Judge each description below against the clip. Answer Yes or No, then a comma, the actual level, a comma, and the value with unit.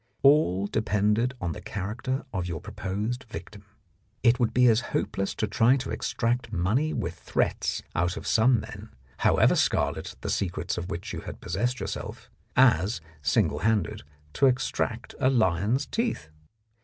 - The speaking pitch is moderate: No, low, 110 Hz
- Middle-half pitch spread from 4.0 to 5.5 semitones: Yes, average, 4.8 semitones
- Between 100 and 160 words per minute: Yes, average, 150 wpm